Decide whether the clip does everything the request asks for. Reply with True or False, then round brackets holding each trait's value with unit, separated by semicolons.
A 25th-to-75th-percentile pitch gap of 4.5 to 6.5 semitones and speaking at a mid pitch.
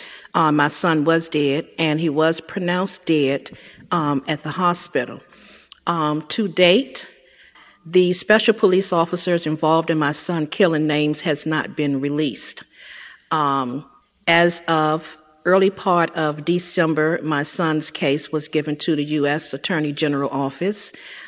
False (2.6 semitones; 155 Hz)